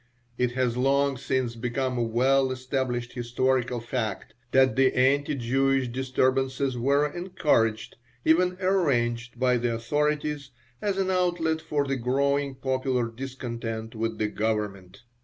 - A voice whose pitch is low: Yes, low, 130 Hz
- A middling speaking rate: No, slow, 130 wpm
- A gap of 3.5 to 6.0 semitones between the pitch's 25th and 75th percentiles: No, average, 2.9 semitones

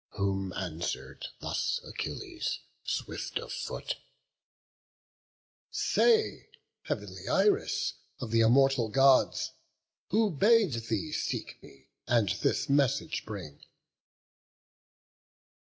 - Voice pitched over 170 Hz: No, low, 130 Hz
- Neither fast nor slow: No, slow, 85 wpm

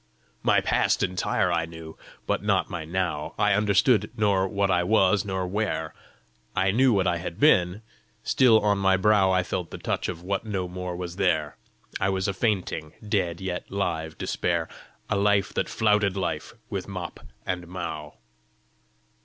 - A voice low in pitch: Yes, very low, 95 Hz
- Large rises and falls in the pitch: No, narrow, 2.6 semitones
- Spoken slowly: No, average, 170 wpm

